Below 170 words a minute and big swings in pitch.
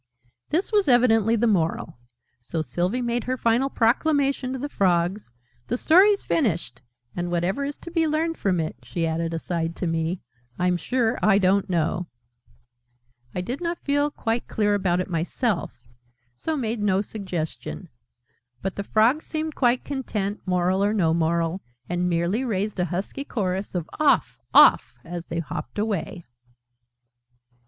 Yes: average, 155 wpm; wide, 6.4 semitones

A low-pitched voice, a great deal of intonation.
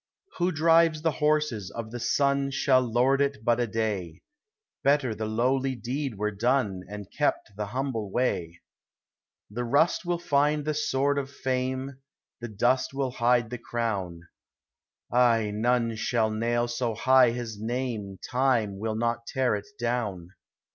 No: low, 120 Hz; average, 3.6 semitones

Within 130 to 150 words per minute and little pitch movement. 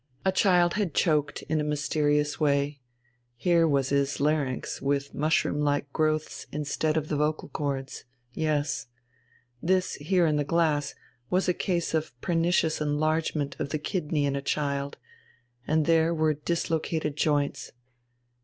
Yes: average, 145 wpm; narrow, 2.1 semitones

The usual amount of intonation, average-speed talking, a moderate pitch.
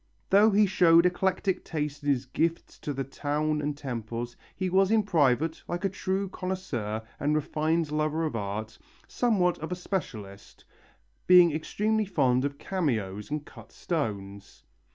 No: wide, 6.2 semitones; average, 155 wpm; medium, 155 Hz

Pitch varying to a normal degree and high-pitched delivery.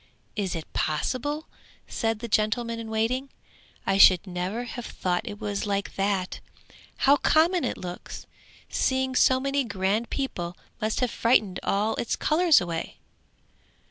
Yes: average, 4.9 semitones; high, 220 Hz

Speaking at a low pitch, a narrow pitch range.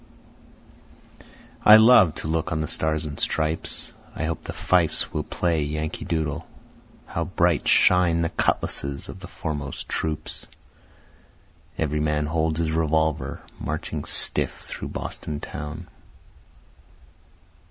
Yes: very low, 80 Hz; narrow, 1.4 semitones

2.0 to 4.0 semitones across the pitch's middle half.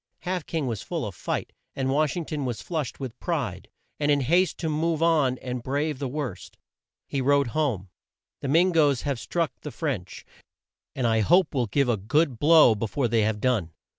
No: average, 4.6 semitones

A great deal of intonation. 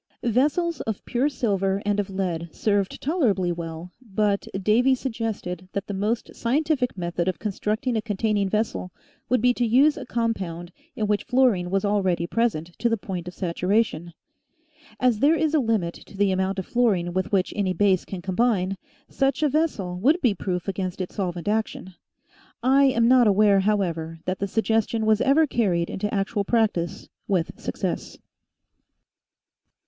No: average, 4.3 semitones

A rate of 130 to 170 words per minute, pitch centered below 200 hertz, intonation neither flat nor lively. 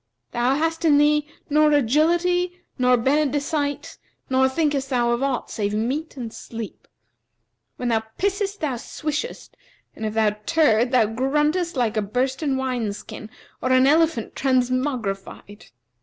No: slow, 135 wpm; very high, 265 Hz; average, 4.3 semitones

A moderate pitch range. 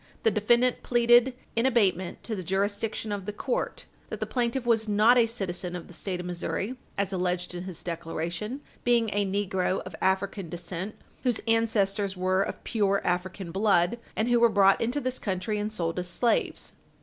Yes: average, 3.9 semitones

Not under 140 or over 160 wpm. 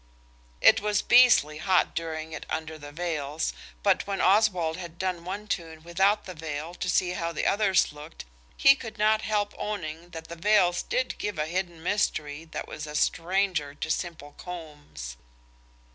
No: average, 170 wpm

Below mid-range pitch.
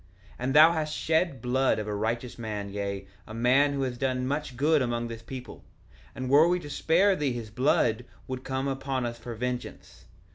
Yes: low, 130 Hz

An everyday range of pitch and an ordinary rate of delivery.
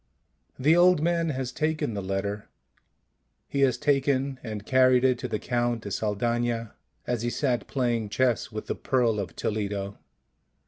Yes: average, 3.7 semitones; average, 155 wpm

